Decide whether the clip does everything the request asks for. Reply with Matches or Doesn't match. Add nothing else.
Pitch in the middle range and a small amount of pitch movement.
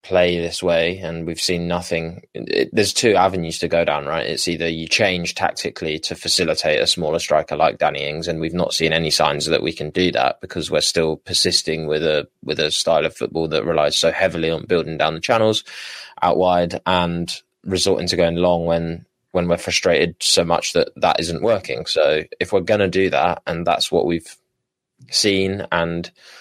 Doesn't match